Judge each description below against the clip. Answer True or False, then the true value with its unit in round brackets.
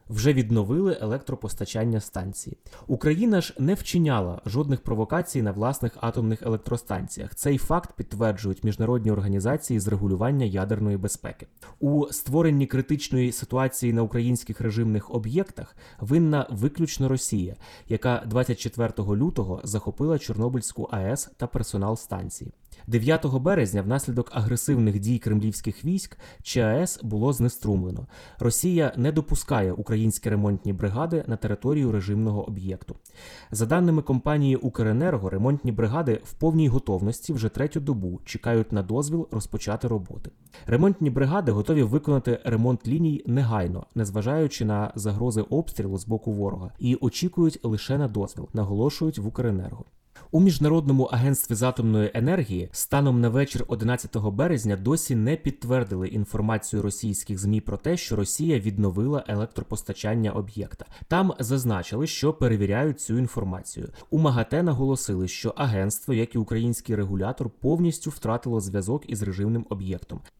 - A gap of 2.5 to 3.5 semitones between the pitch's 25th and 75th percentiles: False (4.7 semitones)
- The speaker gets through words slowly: False (125 wpm)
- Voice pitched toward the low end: True (115 Hz)